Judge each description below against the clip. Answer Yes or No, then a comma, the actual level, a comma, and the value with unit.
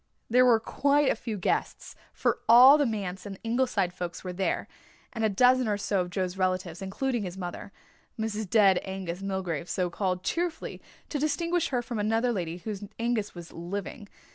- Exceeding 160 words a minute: Yes, average, 180 wpm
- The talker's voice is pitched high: Yes, high, 205 Hz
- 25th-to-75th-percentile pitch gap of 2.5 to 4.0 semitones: No, average, 4.6 semitones